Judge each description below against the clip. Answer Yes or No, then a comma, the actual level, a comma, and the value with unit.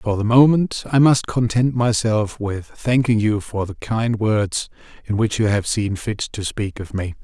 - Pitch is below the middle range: Yes, low, 110 Hz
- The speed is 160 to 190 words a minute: No, average, 200 wpm